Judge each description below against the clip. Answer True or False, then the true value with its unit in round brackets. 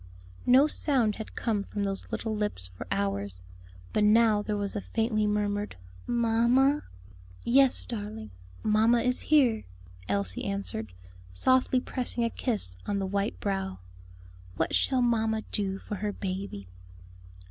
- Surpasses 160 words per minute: False (135 wpm)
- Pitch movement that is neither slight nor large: True (3.4 semitones)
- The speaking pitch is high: True (210 Hz)